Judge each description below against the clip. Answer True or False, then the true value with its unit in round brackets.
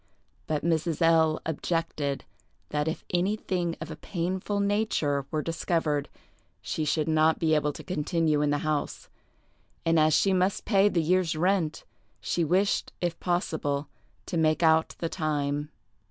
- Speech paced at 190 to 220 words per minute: False (150 wpm)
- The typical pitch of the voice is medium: True (160 Hz)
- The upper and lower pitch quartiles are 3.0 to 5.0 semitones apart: False (2.6 semitones)